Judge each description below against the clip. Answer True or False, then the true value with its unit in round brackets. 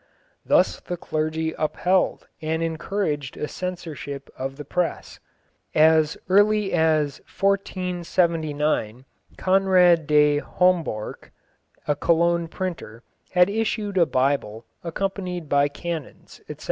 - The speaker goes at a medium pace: False (105 wpm)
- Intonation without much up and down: False (3.6 semitones)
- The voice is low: False (165 Hz)